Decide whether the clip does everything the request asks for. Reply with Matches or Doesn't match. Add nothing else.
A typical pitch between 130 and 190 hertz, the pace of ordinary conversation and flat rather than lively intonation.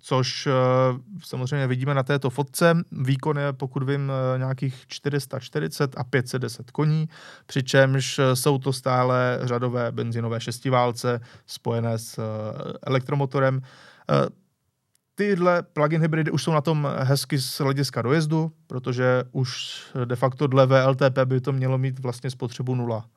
Matches